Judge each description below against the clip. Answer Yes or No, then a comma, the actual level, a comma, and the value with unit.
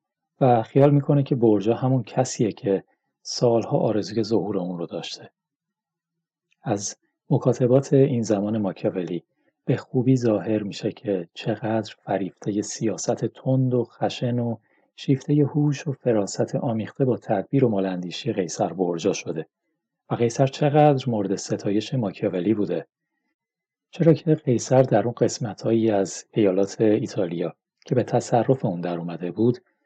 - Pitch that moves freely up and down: No, average, 4.3 semitones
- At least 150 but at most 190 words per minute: No, average, 135 wpm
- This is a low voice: Yes, low, 120 Hz